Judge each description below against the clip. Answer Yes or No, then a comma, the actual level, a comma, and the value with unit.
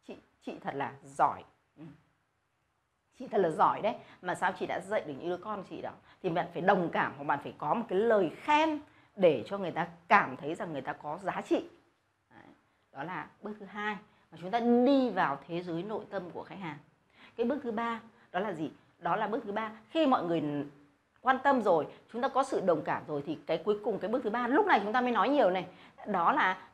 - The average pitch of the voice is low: No, high, 210 Hz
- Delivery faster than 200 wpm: Yes, average, 235 wpm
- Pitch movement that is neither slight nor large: No, wide, 6.6 semitones